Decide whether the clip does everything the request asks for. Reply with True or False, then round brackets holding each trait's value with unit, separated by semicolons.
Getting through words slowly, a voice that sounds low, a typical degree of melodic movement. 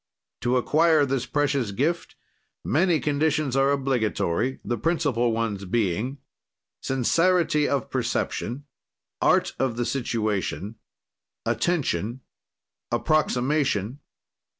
True (90 wpm; 130 Hz; 4.3 semitones)